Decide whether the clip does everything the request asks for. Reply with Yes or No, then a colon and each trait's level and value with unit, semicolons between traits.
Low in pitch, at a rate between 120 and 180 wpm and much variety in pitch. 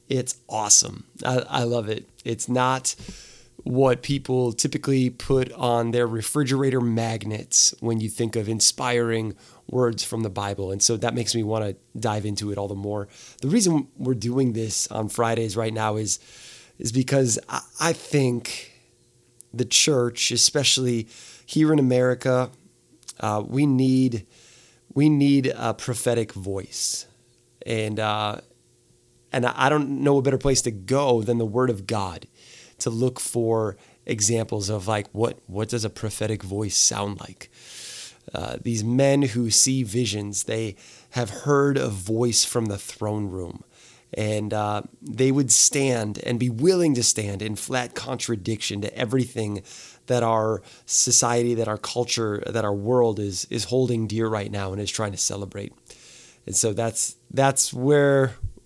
No: low, 115 Hz; average, 155 wpm; average, 2.9 semitones